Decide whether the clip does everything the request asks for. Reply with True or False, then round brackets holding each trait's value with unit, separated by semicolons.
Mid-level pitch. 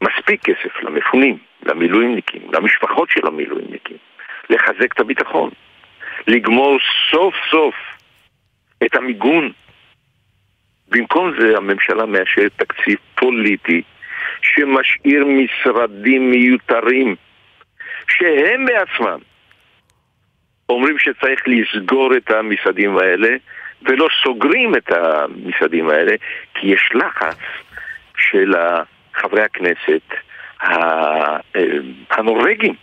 False (130 Hz)